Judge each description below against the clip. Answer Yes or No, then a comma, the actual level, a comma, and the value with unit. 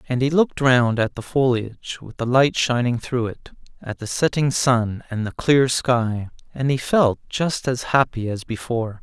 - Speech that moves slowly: No, average, 195 wpm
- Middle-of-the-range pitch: No, low, 125 Hz